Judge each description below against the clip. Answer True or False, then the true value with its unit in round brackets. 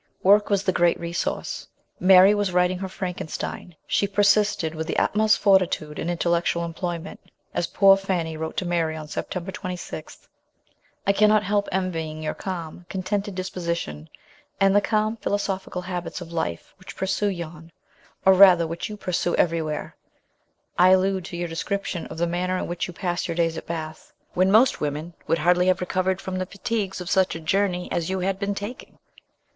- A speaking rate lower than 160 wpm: False (180 wpm)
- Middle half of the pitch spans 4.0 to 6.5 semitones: False (2.5 semitones)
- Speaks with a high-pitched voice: False (180 Hz)